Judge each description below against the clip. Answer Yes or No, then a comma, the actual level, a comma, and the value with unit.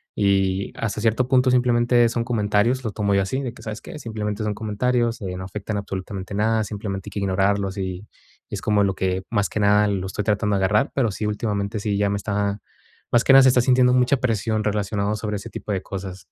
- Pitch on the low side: Yes, low, 105 Hz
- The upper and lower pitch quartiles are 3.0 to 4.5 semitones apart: No, narrow, 2.5 semitones